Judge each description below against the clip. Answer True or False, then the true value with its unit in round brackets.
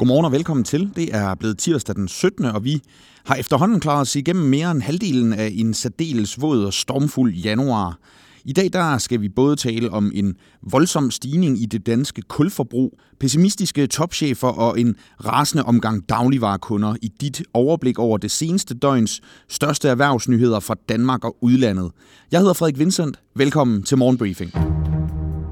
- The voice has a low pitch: True (125 Hz)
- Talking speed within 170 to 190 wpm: False (160 wpm)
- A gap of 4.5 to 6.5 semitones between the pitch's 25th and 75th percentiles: True (5.0 semitones)